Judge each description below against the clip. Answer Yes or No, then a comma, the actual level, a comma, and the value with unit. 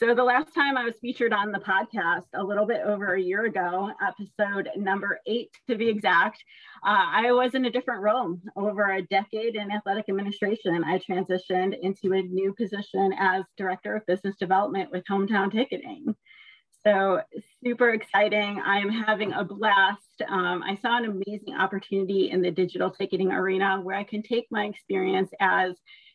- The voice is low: No, high, 200 Hz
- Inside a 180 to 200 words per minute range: No, average, 170 wpm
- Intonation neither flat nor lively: No, narrow, 2.2 semitones